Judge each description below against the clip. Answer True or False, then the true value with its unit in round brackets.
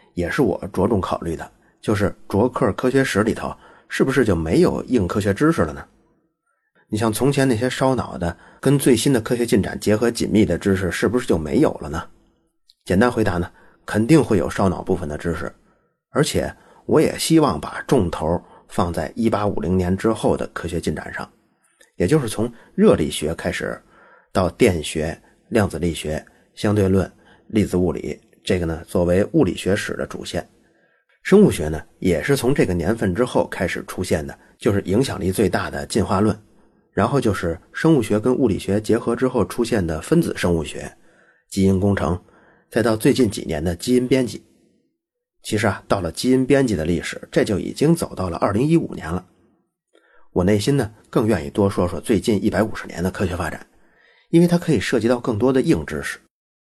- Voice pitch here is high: False (110 Hz)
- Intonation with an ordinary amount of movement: False (5.8 semitones)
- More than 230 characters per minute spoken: True (275 characters per minute)